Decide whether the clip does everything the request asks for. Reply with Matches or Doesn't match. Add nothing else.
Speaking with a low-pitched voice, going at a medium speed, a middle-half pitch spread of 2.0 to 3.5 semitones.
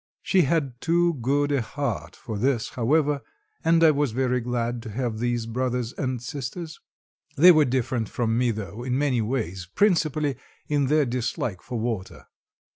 Doesn't match